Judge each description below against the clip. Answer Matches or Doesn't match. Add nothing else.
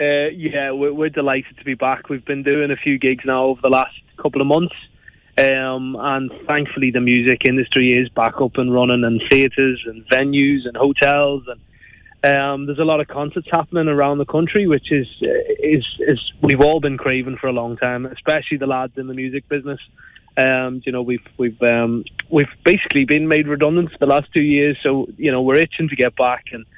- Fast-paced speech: Matches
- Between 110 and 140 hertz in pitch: Matches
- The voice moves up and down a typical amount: Doesn't match